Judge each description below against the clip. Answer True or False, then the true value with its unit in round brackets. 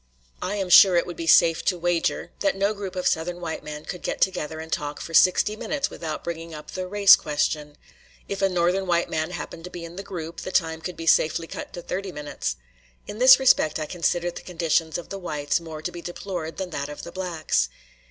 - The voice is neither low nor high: True (170 Hz)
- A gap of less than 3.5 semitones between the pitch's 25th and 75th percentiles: True (2.7 semitones)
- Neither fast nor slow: False (230 wpm)